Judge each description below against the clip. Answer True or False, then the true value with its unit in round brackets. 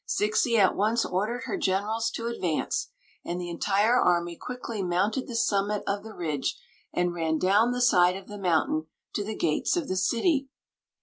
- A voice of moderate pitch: False (200 Hz)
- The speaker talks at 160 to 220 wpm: True (180 wpm)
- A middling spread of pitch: True (4.4 semitones)